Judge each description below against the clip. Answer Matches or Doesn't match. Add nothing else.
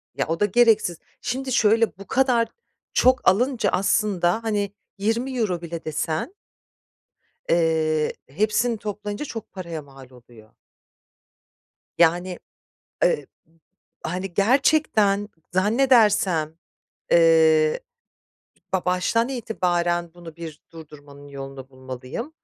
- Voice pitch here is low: Doesn't match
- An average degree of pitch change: Doesn't match